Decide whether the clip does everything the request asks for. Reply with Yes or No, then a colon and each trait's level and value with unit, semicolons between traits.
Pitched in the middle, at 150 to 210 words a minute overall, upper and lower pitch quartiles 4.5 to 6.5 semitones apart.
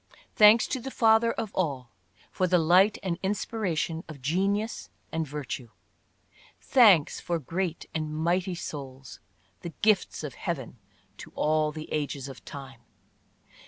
No: medium, 170 Hz; slow, 135 wpm; average, 5.0 semitones